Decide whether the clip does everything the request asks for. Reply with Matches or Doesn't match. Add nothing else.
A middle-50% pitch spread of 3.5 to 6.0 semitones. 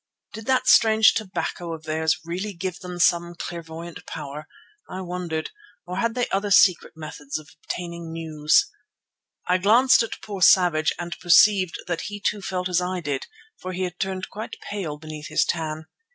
Doesn't match